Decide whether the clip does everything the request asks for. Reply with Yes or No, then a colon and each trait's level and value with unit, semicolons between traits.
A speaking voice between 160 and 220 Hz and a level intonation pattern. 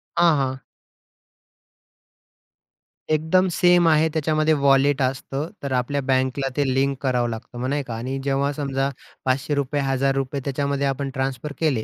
No: medium, 140 Hz; narrow, 1.7 semitones